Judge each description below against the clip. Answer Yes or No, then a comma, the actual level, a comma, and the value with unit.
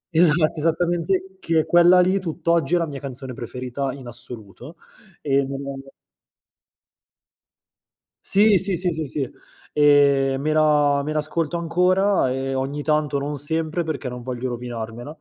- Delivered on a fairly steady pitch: No, average, 3.9 semitones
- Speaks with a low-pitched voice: No, medium, 150 Hz